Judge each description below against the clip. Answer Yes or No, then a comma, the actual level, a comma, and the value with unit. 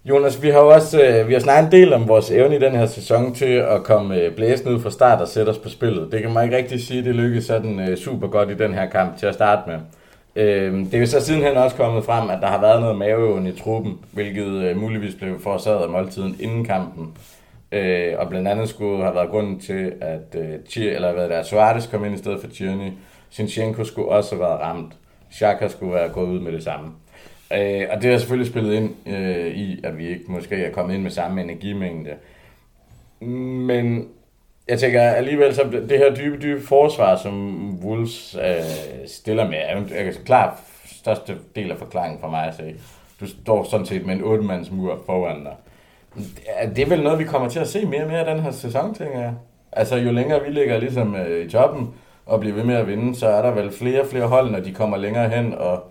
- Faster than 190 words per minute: Yes, average, 220 wpm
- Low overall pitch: Yes, low, 110 Hz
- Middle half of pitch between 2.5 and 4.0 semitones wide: No, average, 4.8 semitones